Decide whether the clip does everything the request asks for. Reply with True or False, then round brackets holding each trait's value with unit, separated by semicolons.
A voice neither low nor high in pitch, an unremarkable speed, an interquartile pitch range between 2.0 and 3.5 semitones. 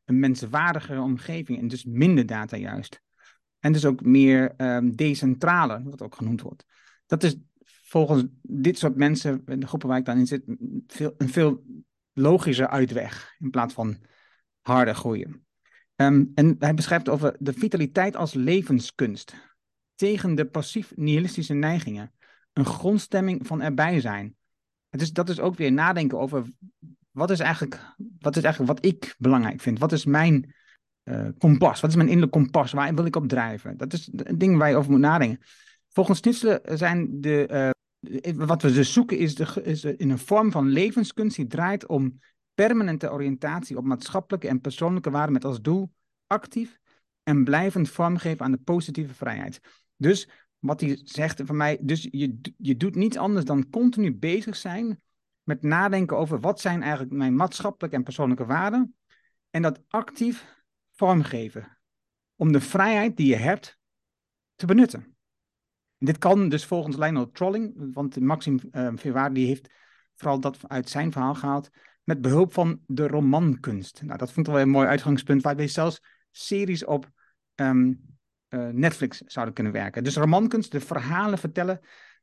False (150 Hz; 165 wpm; 4.8 semitones)